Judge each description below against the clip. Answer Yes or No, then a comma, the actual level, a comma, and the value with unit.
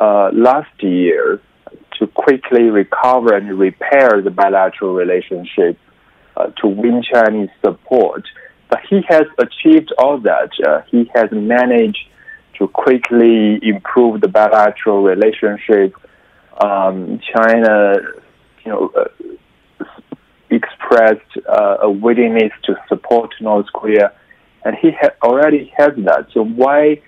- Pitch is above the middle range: No, low, 115 Hz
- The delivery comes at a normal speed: No, slow, 115 wpm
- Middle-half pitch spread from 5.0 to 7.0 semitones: Yes, wide, 5.6 semitones